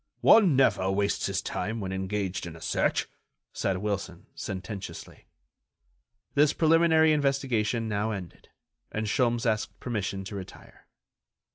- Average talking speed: No, slow, 125 wpm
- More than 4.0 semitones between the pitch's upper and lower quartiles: Yes, average, 5.2 semitones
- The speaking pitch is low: Yes, low, 105 Hz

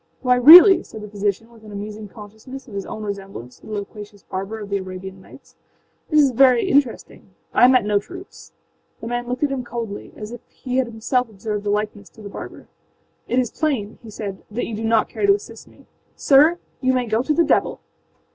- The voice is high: Yes, high, 220 Hz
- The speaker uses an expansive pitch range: No, average, 3.8 semitones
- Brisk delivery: Yes, fast, 220 wpm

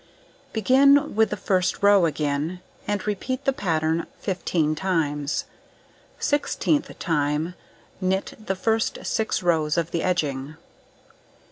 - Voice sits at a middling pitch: Yes, medium, 180 Hz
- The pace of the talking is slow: Yes, slow, 115 wpm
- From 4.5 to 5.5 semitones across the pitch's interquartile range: Yes, average, 5.0 semitones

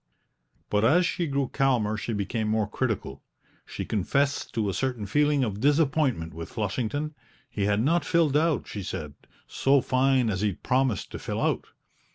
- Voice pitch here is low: Yes, low, 125 Hz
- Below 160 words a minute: No, average, 170 wpm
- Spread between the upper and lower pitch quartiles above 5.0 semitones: Yes, wide, 5.4 semitones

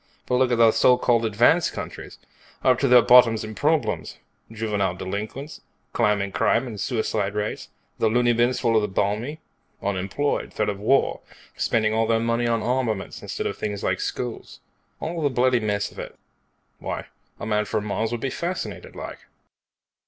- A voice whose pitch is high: No, low, 115 Hz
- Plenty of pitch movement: No, average, 3.1 semitones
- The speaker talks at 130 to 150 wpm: No, average, 175 wpm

